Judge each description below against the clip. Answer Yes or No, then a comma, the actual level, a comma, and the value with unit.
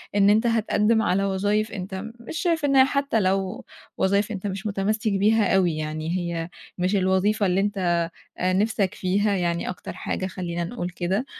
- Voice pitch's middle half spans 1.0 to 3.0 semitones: Yes, average, 2.7 semitones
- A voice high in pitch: Yes, high, 195 Hz